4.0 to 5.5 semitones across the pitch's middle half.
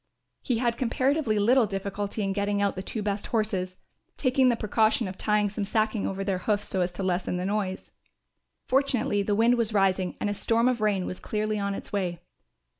No: average, 2.7 semitones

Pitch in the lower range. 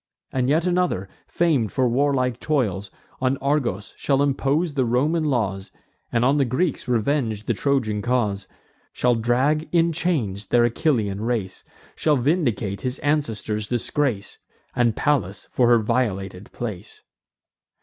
Yes: low, 125 Hz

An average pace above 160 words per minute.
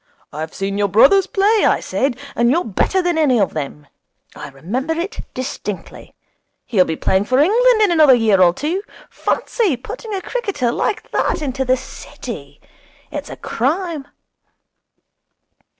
No: average, 150 wpm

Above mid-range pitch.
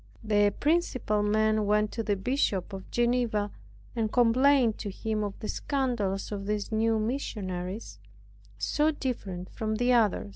Yes: high, 215 Hz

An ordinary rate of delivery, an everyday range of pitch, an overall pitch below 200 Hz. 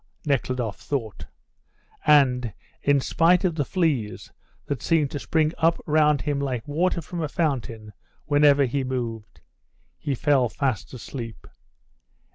No: slow, 130 wpm; average, 3.6 semitones; medium, 140 Hz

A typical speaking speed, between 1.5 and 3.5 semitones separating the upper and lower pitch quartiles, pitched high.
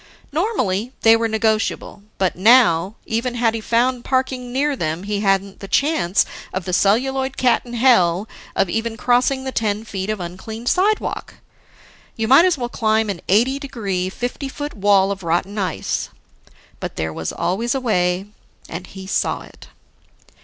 No: average, 165 wpm; average, 4.8 semitones; high, 220 Hz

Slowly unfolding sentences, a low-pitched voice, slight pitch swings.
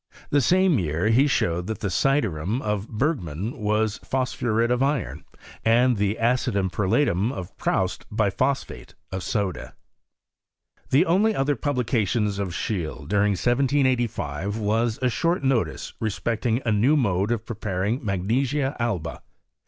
No: slow, 130 wpm; low, 110 Hz; average, 4.6 semitones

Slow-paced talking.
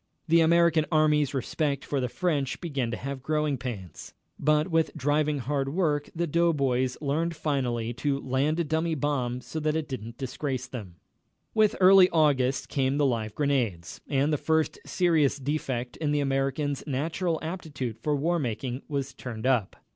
No: average, 170 wpm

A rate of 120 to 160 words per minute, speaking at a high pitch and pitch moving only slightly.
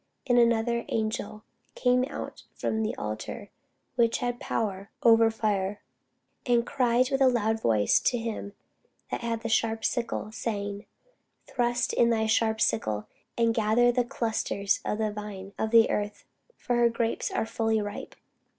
Yes: average, 155 wpm; high, 225 Hz; narrow, 2.2 semitones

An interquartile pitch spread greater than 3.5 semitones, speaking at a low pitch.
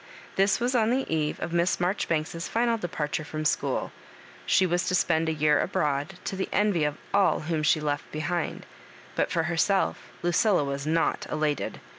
No: average, 3.9 semitones; medium, 165 Hz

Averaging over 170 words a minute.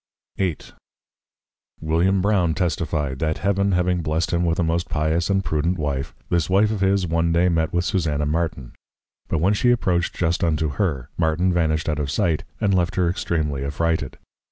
Yes: average, 180 wpm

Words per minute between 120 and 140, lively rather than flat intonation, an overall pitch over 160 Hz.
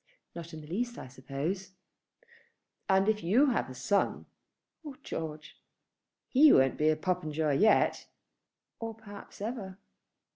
Yes: slow, 135 wpm; wide, 6.1 semitones; high, 190 Hz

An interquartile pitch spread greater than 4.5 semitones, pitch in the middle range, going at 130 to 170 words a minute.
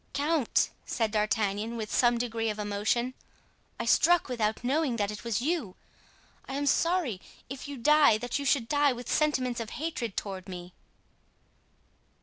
No: average, 4.9 semitones; high, 240 Hz; average, 155 wpm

